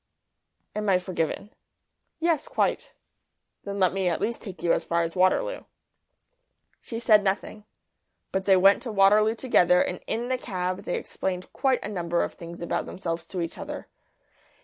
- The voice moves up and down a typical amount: Yes, average, 3.4 semitones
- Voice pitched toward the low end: No, high, 190 Hz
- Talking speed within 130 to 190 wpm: Yes, average, 170 wpm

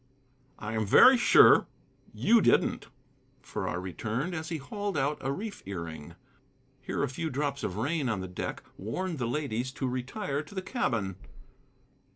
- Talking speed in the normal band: Yes, average, 160 wpm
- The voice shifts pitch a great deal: Yes, wide, 7.4 semitones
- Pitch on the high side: No, low, 135 Hz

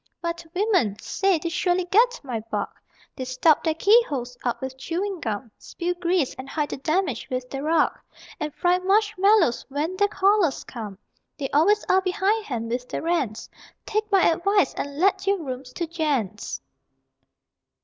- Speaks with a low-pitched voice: No, very high, 335 Hz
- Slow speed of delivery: No, average, 160 wpm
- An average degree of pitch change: No, wide, 6.7 semitones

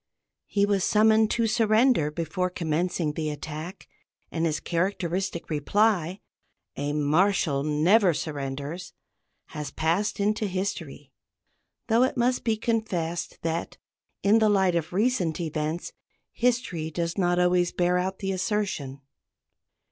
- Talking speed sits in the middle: No, slow, 130 wpm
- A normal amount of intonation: Yes, average, 4.7 semitones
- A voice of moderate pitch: Yes, medium, 180 Hz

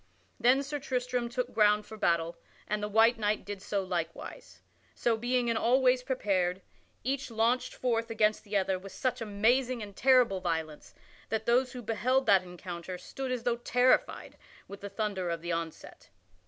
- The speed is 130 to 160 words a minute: No, average, 175 wpm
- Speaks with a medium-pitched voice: No, high, 220 Hz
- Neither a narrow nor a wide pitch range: Yes, average, 4.5 semitones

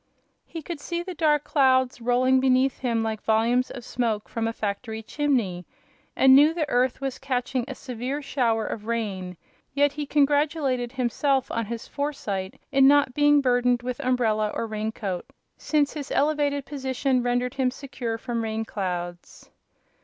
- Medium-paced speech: Yes, average, 160 wpm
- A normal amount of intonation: Yes, average, 3.7 semitones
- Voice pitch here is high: Yes, very high, 250 Hz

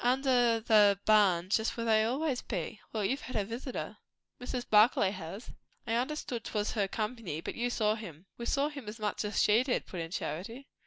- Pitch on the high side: Yes, high, 220 Hz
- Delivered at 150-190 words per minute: No, average, 200 wpm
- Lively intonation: No, average, 3.2 semitones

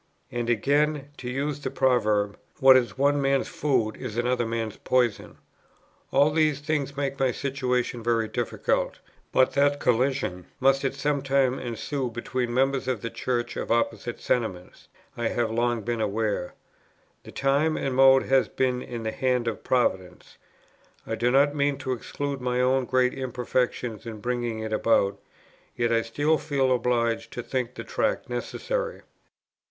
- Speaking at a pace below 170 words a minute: Yes, average, 160 wpm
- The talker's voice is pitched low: Yes, low, 125 Hz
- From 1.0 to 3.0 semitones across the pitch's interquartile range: Yes, average, 2.7 semitones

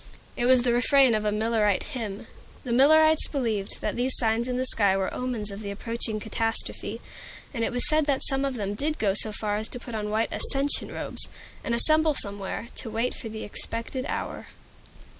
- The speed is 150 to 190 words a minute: No, average, 200 wpm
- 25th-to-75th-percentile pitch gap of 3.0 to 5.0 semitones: Yes, average, 3.5 semitones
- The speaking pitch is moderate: No, high, 230 Hz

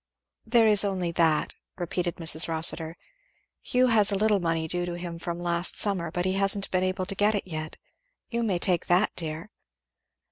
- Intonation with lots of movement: No, average, 3.0 semitones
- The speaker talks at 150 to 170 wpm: No, average, 185 wpm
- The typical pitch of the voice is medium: Yes, medium, 180 Hz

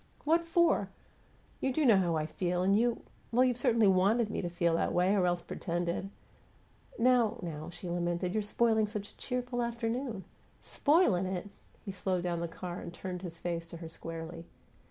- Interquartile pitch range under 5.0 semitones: No, average, 5.3 semitones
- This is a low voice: No, high, 190 Hz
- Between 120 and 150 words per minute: No, average, 190 wpm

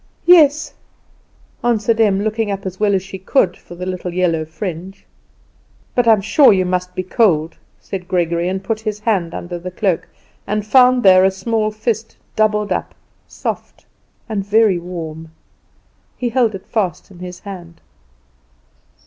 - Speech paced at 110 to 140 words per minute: No, average, 155 wpm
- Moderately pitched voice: No, high, 195 Hz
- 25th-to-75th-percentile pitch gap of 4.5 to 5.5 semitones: No, average, 3.3 semitones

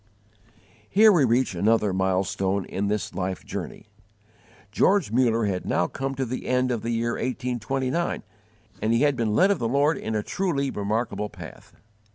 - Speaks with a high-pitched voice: No, low, 115 Hz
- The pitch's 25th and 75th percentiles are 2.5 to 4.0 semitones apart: No, average, 4.5 semitones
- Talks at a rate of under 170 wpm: No, average, 175 wpm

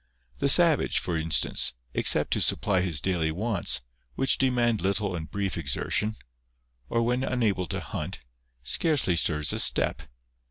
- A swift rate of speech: No, average, 145 wpm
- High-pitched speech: No, low, 100 Hz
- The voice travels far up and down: Yes, wide, 6.2 semitones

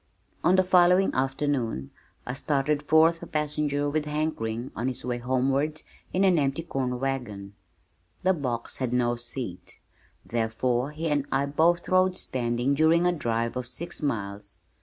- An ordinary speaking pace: Yes, average, 160 wpm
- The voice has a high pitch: No, low, 135 Hz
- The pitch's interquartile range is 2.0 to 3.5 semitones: No, average, 4.6 semitones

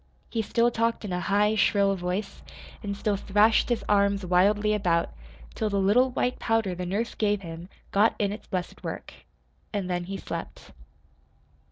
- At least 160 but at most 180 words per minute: Yes, average, 170 wpm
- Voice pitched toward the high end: Yes, high, 200 Hz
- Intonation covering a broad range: No, narrow, 2.6 semitones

